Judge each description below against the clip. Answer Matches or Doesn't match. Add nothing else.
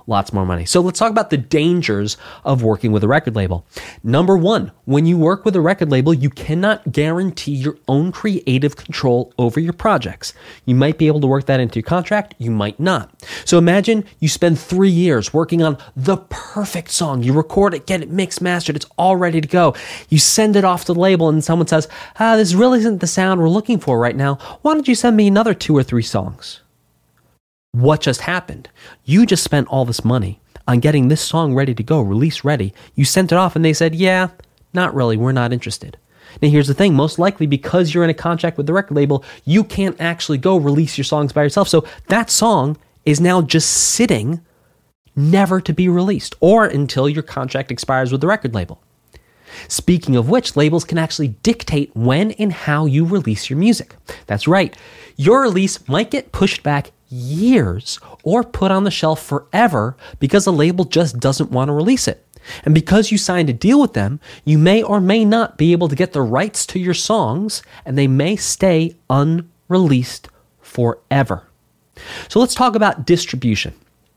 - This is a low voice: Doesn't match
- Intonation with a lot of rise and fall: Matches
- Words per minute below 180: Doesn't match